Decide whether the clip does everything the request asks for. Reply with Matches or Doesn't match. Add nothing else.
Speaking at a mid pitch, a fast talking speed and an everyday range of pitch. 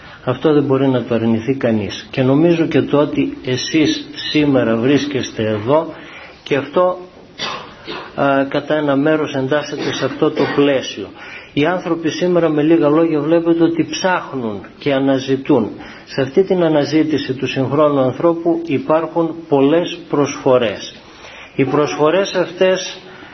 Doesn't match